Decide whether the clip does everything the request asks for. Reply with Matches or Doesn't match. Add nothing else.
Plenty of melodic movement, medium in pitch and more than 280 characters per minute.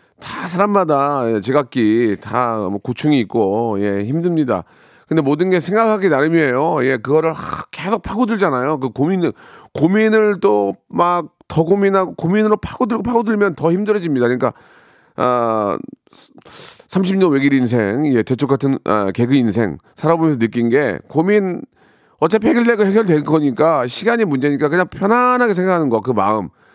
Matches